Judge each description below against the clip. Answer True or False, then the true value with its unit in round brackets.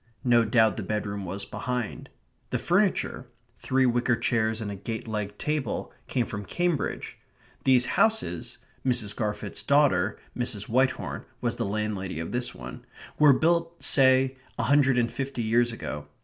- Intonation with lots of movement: False (4.0 semitones)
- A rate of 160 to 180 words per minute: False (150 wpm)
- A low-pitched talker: True (120 Hz)